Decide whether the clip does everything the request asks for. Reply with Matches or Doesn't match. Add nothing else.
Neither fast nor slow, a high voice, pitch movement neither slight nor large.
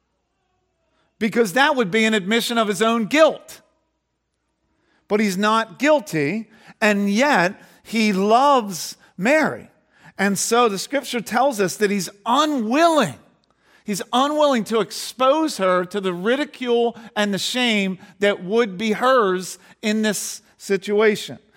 Doesn't match